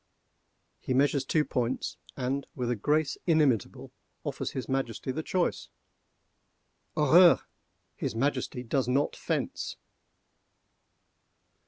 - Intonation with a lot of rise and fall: No, average, 3.1 semitones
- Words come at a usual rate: No, slow, 105 wpm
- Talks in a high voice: No, low, 135 Hz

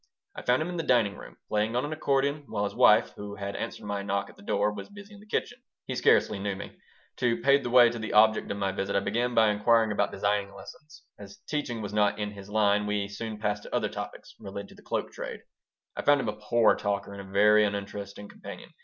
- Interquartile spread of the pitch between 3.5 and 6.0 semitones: No, average, 3.0 semitones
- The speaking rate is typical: No, fast, 245 wpm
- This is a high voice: No, low, 105 Hz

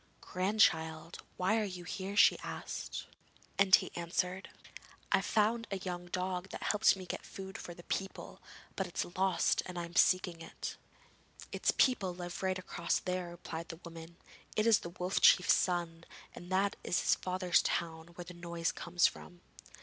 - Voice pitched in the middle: Yes, medium, 180 Hz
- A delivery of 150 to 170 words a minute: No, average, 180 wpm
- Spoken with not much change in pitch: Yes, narrow, 1.8 semitones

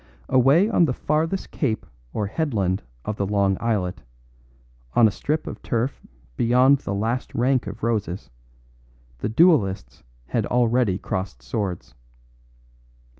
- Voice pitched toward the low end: Yes, low, 115 Hz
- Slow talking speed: Yes, slow, 125 wpm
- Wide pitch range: No, average, 5.0 semitones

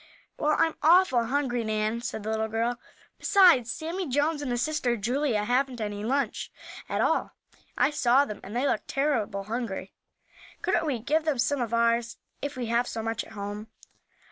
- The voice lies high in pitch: Yes, high, 240 Hz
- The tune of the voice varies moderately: Yes, average, 4.4 semitones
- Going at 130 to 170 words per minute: No, average, 180 wpm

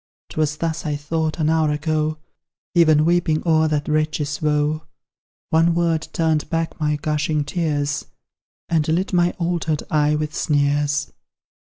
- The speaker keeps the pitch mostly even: Yes, narrow, 1.5 semitones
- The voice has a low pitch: No, medium, 155 Hz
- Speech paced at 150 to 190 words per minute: No, average, 140 wpm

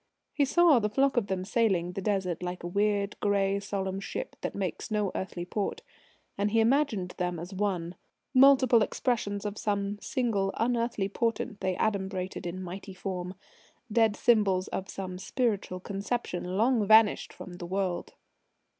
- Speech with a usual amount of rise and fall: Yes, average, 3.2 semitones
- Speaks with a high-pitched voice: Yes, high, 200 Hz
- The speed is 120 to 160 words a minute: Yes, average, 155 wpm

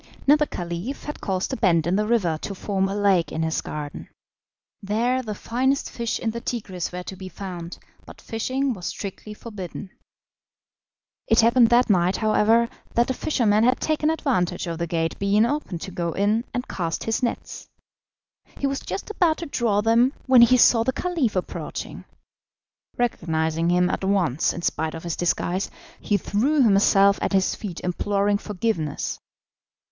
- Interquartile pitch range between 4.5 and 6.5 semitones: Yes, average, 5.0 semitones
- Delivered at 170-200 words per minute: Yes, average, 175 wpm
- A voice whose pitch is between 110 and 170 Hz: No, high, 205 Hz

